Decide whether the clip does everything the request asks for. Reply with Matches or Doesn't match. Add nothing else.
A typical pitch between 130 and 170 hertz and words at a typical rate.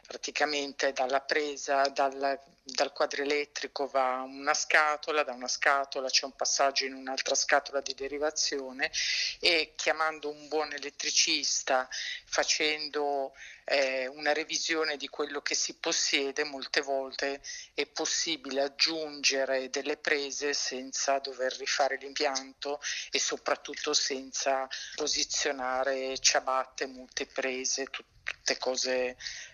Doesn't match